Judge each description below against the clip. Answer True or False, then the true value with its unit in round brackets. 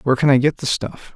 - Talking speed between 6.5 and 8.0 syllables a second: True (6.7 syllables/s)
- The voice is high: False (135 Hz)